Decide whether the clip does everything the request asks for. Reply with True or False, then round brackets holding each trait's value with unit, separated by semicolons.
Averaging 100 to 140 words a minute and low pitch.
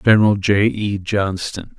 True (135 wpm; 100 Hz)